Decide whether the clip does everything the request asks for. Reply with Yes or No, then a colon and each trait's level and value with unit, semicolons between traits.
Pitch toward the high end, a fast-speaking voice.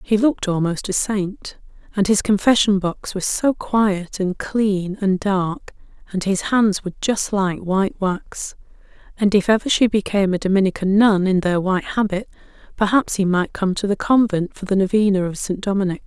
No: high, 195 Hz; average, 180 wpm